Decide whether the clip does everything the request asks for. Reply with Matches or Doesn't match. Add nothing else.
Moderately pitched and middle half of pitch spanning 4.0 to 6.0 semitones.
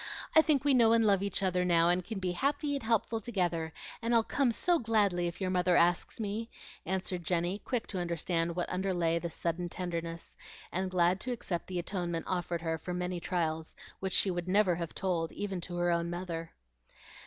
Doesn't match